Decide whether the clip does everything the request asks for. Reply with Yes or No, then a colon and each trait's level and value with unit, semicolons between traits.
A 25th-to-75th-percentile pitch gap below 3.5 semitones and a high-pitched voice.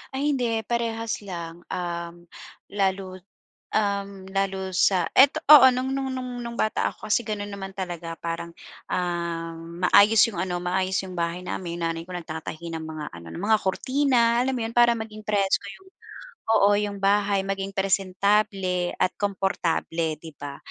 No: average, 4.1 semitones; high, 195 Hz